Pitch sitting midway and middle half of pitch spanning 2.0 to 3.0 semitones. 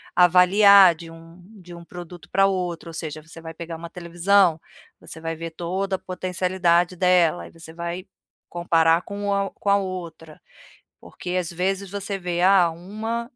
Yes: medium, 180 Hz; narrow, 2.4 semitones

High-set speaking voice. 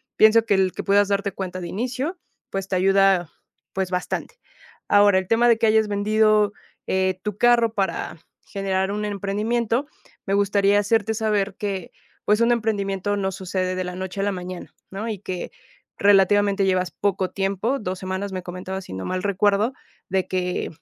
Yes: high, 200 Hz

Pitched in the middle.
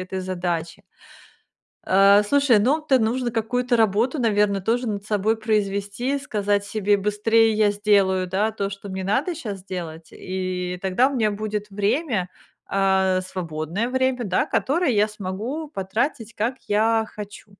No: high, 210 Hz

